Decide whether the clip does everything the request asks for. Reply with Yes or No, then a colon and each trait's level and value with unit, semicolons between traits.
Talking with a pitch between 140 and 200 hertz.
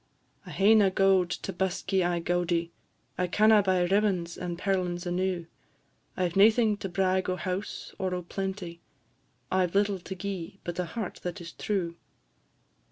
Yes: medium, 185 Hz